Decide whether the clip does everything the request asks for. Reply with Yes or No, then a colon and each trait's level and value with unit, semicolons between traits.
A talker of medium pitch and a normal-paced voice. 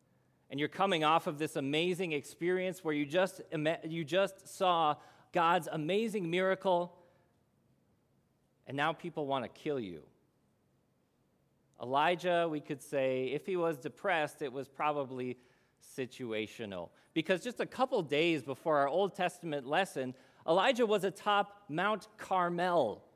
No: medium, 165 Hz; slow, 130 wpm